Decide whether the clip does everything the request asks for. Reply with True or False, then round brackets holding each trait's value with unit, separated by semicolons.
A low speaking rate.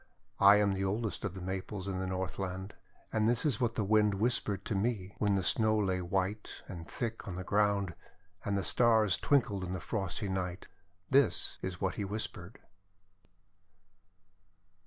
False (180 wpm)